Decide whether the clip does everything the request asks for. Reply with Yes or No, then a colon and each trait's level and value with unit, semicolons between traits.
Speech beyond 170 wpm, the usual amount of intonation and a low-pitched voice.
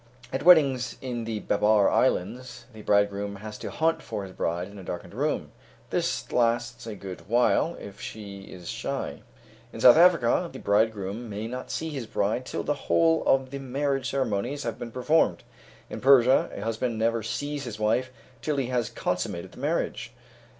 Yes: average, 180 wpm; average, 4.5 semitones; low, 115 Hz